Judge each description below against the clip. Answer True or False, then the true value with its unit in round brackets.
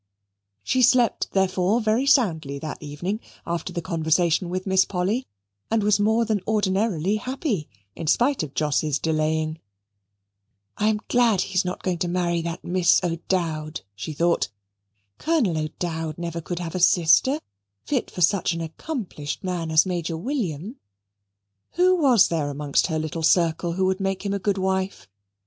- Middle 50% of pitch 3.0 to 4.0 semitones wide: False (4.5 semitones)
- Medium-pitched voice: True (180 Hz)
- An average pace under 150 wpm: False (160 wpm)